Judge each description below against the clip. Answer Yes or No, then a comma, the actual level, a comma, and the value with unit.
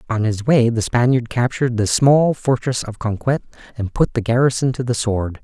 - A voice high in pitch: No, low, 120 Hz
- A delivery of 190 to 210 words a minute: Yes, average, 200 wpm